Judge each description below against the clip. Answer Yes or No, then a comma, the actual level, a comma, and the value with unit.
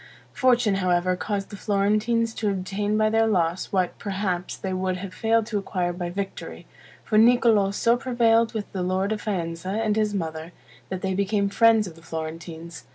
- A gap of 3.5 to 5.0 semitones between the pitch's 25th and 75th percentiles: No, average, 3.1 semitones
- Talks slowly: No, average, 180 wpm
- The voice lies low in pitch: No, high, 200 Hz